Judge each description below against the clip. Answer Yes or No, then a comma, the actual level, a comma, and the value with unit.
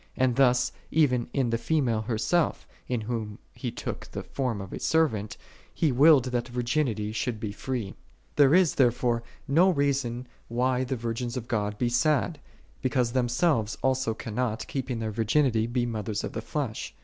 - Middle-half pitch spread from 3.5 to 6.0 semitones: No, average, 3.0 semitones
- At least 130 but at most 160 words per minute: No, average, 170 wpm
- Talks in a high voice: No, low, 125 Hz